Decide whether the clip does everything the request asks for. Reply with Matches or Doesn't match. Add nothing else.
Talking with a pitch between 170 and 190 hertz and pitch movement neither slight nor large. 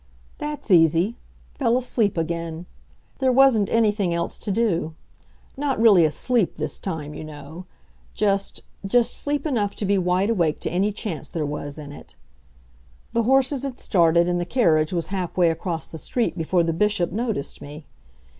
Doesn't match